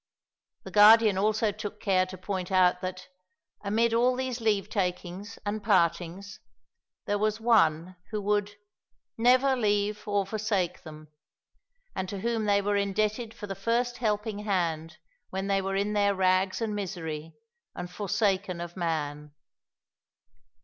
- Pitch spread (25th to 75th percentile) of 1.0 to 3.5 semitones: Yes, narrow, 2.6 semitones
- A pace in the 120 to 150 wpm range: Yes, average, 140 wpm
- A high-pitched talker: Yes, high, 200 Hz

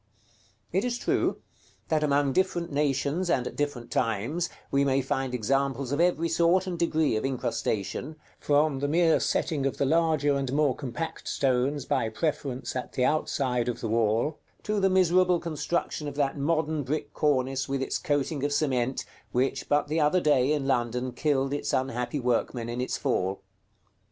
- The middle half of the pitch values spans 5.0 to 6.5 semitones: No, average, 3.4 semitones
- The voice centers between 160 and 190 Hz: No, medium, 140 Hz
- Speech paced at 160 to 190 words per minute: Yes, average, 170 wpm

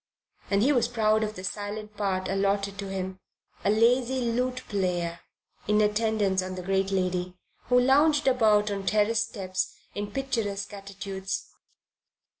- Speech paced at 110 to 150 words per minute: Yes, average, 145 wpm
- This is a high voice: Yes, high, 205 Hz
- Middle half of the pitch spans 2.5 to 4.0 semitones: Yes, average, 2.9 semitones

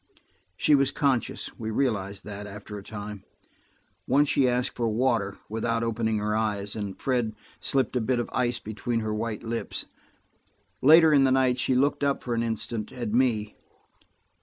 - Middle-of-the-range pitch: No, low, 115 Hz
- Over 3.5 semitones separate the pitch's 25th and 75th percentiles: No, average, 3.2 semitones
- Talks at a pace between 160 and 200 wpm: Yes, average, 170 wpm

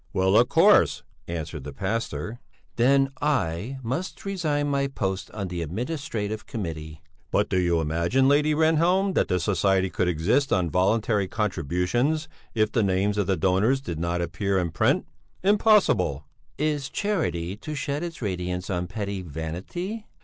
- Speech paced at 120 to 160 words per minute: Yes, average, 150 wpm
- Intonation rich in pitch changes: Yes, wide, 7.9 semitones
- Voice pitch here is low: Yes, low, 100 Hz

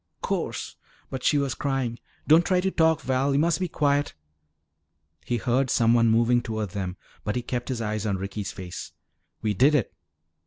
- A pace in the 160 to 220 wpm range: Yes, average, 180 wpm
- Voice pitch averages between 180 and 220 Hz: No, low, 125 Hz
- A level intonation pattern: No, average, 4.6 semitones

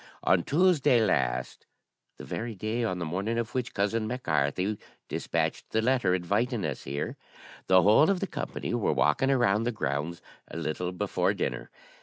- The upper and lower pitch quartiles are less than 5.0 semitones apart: No, average, 5.3 semitones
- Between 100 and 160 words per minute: No, average, 170 wpm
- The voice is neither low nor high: No, low, 105 Hz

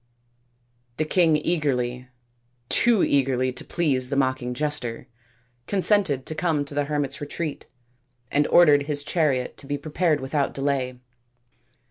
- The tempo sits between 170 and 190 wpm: No, slow, 135 wpm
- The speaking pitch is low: No, medium, 145 Hz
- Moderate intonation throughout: Yes, average, 3.0 semitones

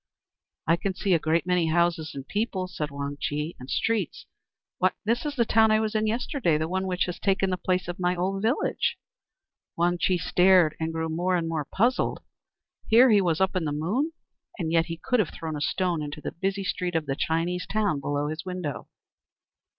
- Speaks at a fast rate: Yes, fast, 210 wpm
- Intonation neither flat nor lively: Yes, average, 3.3 semitones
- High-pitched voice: No, medium, 180 Hz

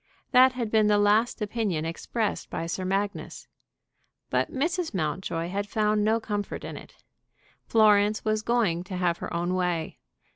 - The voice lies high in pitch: Yes, high, 205 Hz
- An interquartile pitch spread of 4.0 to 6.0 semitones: No, average, 3.4 semitones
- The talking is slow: No, average, 155 wpm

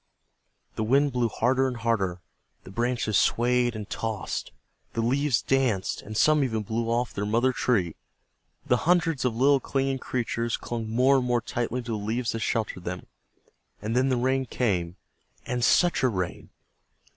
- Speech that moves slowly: No, average, 170 wpm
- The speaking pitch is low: Yes, low, 120 Hz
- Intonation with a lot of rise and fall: No, average, 2.9 semitones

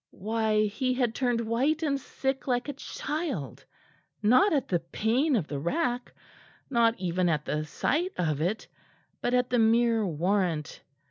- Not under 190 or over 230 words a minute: No, average, 155 wpm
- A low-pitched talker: No, high, 230 Hz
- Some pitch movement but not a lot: No, wide, 6.4 semitones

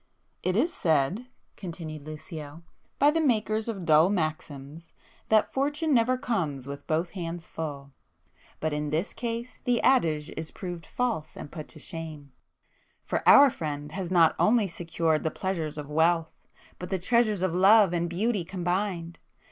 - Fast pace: No, average, 150 wpm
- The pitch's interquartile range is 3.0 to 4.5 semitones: No, wide, 5.6 semitones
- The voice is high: No, medium, 170 Hz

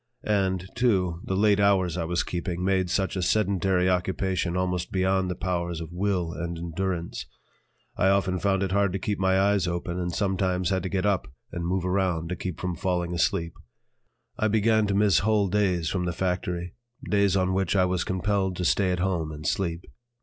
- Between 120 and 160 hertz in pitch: No, very low, 95 Hz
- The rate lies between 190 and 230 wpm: Yes, average, 195 wpm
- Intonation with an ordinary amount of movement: No, narrow, 1.9 semitones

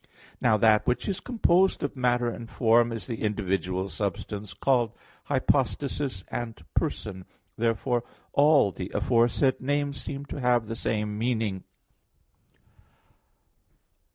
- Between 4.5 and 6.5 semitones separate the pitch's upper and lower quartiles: No, average, 4.0 semitones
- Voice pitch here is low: Yes, low, 120 Hz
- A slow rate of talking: Yes, slow, 120 wpm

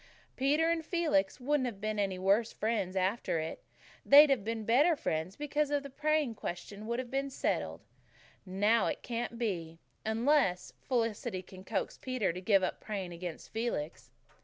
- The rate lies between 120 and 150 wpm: No, average, 165 wpm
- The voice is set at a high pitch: Yes, high, 225 Hz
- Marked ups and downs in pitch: Yes, wide, 6.2 semitones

